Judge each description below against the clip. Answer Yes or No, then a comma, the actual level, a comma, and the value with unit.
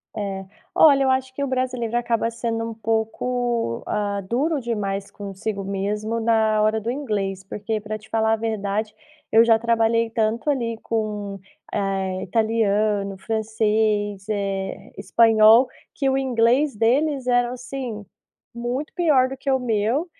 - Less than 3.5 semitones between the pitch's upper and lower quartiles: Yes, average, 2.8 semitones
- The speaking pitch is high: Yes, high, 225 Hz